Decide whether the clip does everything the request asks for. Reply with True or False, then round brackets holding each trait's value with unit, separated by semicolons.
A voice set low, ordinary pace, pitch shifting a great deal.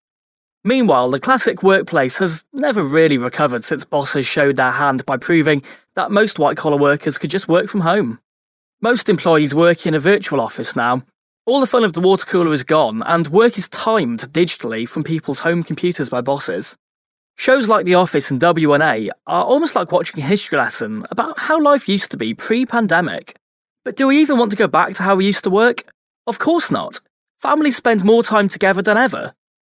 False (180 Hz; 195 wpm; 7.0 semitones)